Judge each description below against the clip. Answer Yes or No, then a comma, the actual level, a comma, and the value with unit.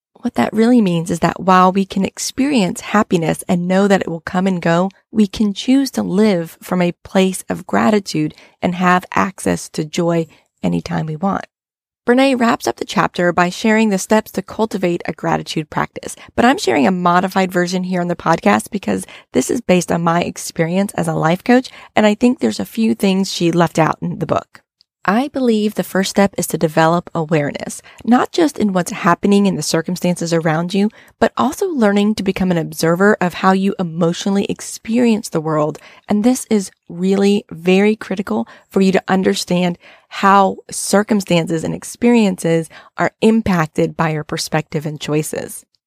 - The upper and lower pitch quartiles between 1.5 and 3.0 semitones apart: No, average, 3.9 semitones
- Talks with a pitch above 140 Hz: Yes, high, 190 Hz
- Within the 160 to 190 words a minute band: Yes, average, 180 wpm